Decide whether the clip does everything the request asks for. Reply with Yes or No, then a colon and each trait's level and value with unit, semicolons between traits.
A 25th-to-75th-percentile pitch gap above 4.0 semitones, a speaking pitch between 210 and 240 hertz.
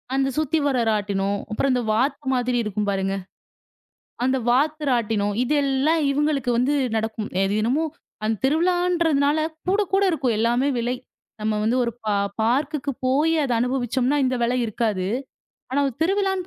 No: average, 5.0 semitones; very high, 255 Hz